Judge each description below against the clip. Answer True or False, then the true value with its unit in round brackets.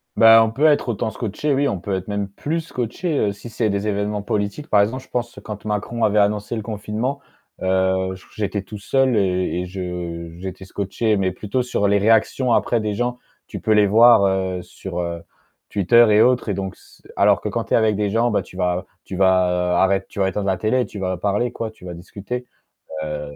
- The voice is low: True (105 Hz)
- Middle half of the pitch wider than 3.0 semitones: True (3.5 semitones)